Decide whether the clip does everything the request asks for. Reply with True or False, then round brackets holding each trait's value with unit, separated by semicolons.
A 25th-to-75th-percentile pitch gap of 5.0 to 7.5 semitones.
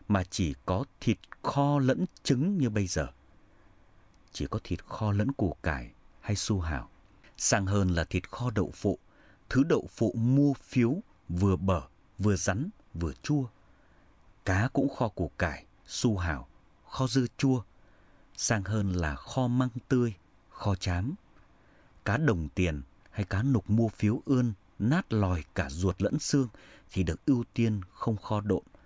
True (5.3 semitones)